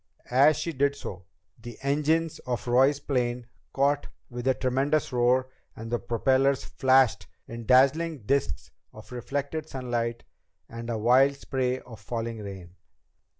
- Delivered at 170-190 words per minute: No, average, 140 wpm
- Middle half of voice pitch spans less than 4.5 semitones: Yes, average, 2.9 semitones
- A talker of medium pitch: No, low, 130 Hz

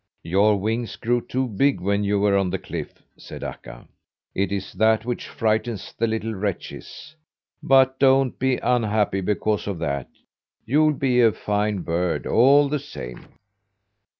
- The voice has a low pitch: Yes, low, 110 Hz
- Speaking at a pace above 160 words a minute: No, average, 150 wpm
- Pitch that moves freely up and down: No, average, 4.0 semitones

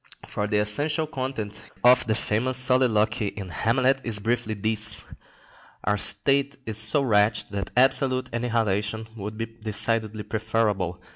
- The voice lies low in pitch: Yes, low, 110 Hz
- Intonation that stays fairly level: No, average, 3.4 semitones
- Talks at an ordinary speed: No, slow, 130 wpm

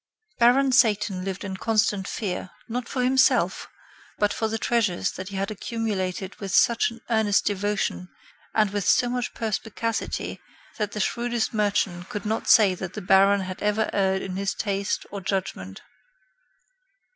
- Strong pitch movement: No, average, 2.8 semitones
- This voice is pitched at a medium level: No, high, 205 Hz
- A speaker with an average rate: Yes, average, 155 wpm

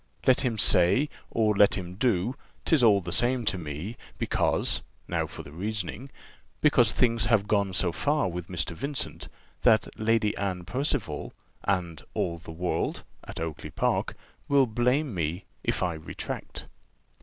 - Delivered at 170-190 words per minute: No, average, 155 wpm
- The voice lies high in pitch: No, low, 105 Hz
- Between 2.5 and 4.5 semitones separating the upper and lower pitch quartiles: No, wide, 5.6 semitones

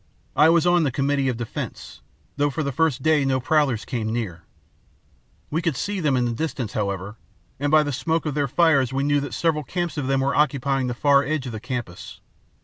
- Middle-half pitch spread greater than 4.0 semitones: No, average, 3.7 semitones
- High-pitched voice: No, medium, 140 Hz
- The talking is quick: Yes, fast, 215 wpm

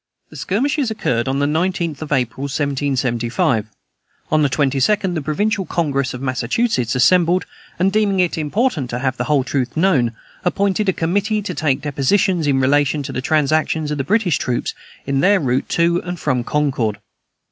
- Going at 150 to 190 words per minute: Yes, average, 170 wpm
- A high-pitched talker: No, medium, 150 Hz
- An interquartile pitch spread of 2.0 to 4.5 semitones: No, wide, 5.6 semitones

